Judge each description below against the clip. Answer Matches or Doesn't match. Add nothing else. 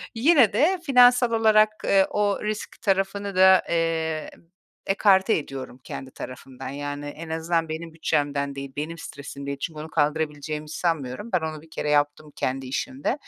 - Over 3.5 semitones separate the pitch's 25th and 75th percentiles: Matches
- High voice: Doesn't match